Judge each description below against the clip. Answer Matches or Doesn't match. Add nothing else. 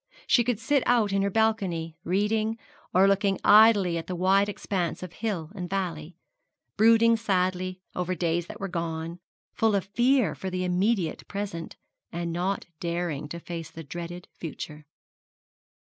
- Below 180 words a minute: Matches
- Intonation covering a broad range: Doesn't match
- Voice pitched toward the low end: Doesn't match